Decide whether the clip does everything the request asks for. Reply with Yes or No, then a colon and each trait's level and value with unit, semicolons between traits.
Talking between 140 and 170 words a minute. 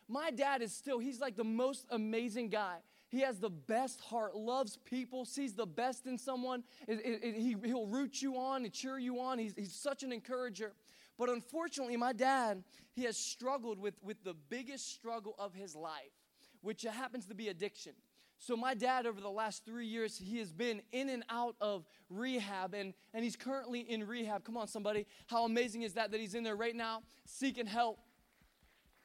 No: average, 200 wpm